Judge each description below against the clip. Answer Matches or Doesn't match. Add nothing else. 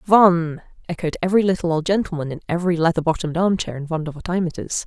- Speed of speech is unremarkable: Matches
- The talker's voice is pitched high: Doesn't match